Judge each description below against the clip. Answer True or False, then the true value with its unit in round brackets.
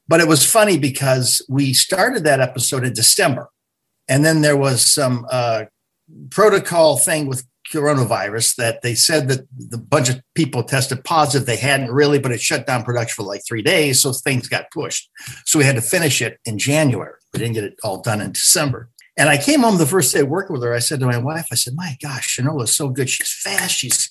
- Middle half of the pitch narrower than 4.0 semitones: True (3.6 semitones)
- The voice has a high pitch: False (135 Hz)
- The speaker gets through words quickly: True (225 wpm)